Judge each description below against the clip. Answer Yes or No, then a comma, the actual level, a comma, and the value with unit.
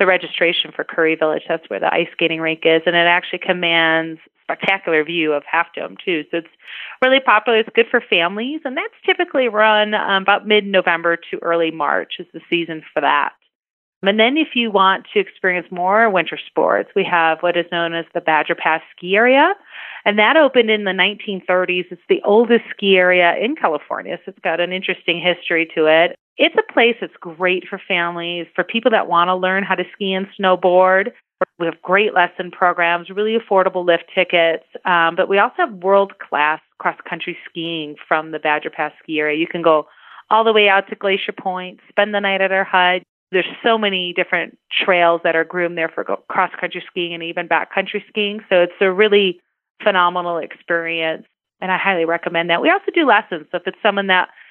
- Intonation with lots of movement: No, average, 3.1 semitones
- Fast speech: No, average, 195 wpm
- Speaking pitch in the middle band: Yes, medium, 180 Hz